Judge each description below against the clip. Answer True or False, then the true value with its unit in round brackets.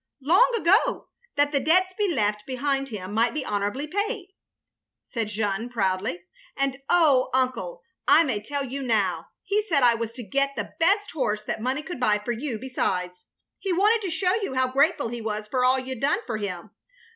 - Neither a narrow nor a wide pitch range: False (6.9 semitones)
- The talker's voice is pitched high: True (260 Hz)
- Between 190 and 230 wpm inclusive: True (205 wpm)